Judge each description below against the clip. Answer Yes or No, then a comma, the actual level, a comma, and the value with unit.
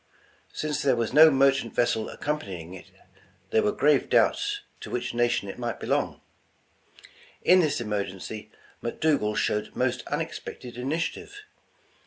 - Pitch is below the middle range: Yes, low, 125 Hz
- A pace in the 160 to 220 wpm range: No, average, 140 wpm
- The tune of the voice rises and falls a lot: Yes, wide, 5.9 semitones